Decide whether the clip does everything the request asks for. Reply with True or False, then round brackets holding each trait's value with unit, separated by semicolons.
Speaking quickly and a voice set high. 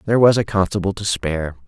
False (215 wpm; 95 Hz)